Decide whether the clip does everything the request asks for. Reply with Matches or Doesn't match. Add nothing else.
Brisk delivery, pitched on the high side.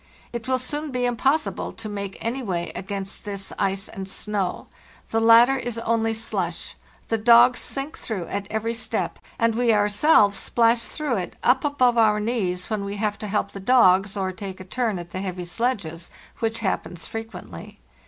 Doesn't match